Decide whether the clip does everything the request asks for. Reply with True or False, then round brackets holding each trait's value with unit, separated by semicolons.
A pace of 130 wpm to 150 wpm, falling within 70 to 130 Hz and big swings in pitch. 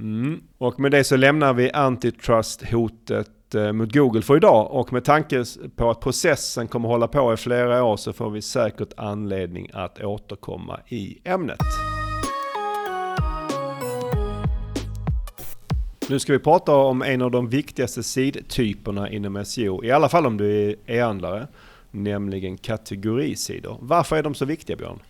False (145 wpm; 120 Hz; 4.7 semitones)